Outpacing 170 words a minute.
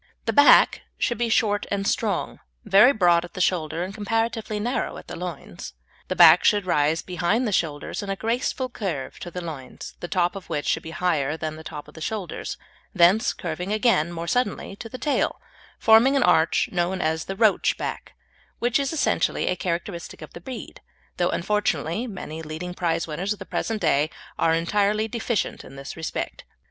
Yes: average, 190 wpm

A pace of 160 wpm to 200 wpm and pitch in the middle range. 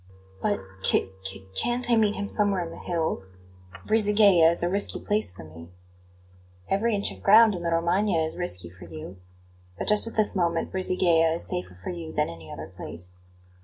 Yes: average, 190 wpm; medium, 170 Hz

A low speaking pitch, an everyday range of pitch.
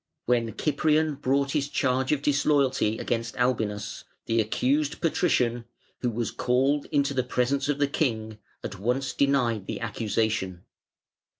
Yes: low, 130 Hz; average, 3.7 semitones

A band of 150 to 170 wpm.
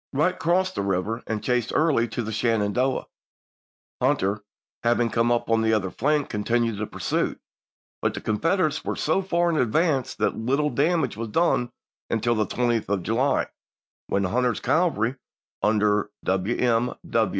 Yes: average, 160 wpm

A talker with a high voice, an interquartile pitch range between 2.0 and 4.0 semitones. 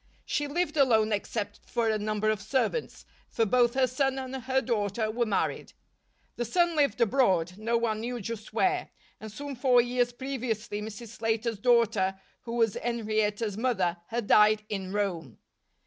Yes: high, 230 Hz; average, 3.1 semitones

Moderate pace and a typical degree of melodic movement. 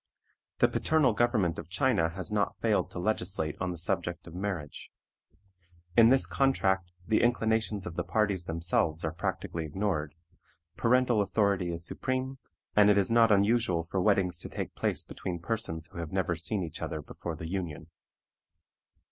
Yes: average, 165 wpm; average, 4.7 semitones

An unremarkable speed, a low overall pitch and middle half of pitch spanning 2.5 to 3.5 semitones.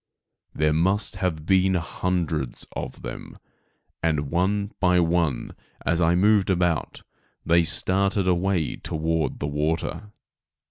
No: slow, 120 wpm; very low, 85 Hz; average, 2.9 semitones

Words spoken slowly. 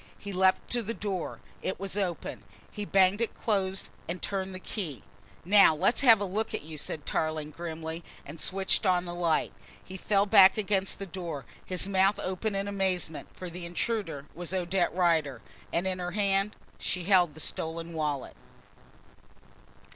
No: average, 170 wpm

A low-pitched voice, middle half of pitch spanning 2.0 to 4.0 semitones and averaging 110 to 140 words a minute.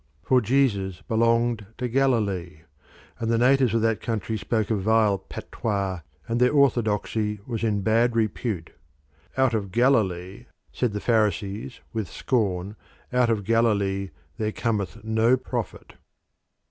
Yes: low, 110 Hz; average, 2.9 semitones; slow, 135 wpm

